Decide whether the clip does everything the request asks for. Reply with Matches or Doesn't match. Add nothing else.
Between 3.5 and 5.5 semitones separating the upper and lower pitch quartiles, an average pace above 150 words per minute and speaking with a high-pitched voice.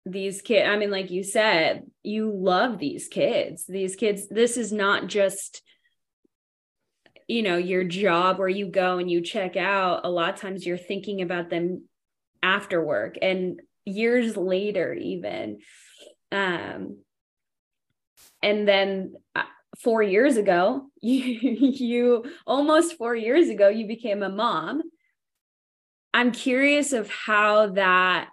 Doesn't match